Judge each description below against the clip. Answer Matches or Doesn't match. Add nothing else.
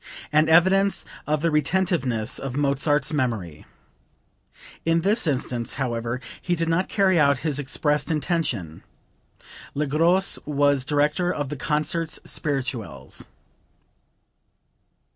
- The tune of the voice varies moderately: Matches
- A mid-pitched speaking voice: Matches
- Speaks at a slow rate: Matches